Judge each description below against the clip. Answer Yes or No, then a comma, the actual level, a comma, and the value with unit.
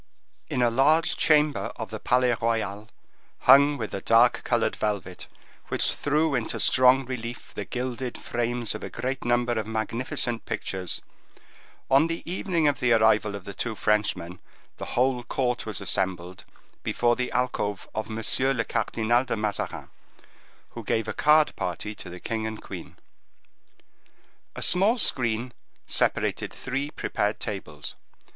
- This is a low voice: Yes, low, 120 Hz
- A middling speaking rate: Yes, average, 150 wpm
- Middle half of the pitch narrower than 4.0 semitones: Yes, average, 3.2 semitones